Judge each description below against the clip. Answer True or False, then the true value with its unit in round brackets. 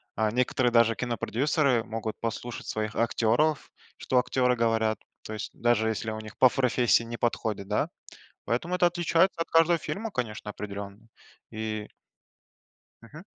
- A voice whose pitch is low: True (115 Hz)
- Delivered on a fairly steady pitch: False (3.1 semitones)